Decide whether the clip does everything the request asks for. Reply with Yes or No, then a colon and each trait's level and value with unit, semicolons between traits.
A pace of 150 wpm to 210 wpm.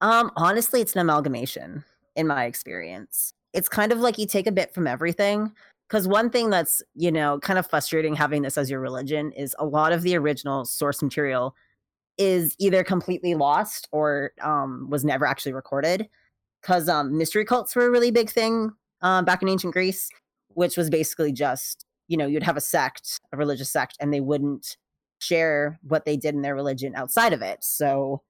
Yes: average, 195 wpm